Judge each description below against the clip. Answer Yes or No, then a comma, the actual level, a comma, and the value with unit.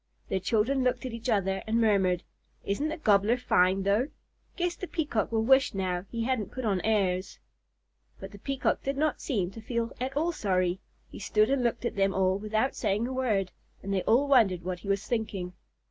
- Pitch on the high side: Yes, high, 220 Hz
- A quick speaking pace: Yes, fast, 210 wpm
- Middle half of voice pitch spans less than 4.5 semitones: No, average, 4.8 semitones